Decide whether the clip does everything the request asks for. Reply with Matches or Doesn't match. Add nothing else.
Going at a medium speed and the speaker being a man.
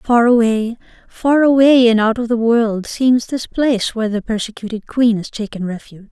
Doesn't match